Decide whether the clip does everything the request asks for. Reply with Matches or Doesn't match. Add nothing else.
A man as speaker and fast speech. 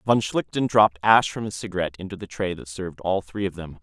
Matches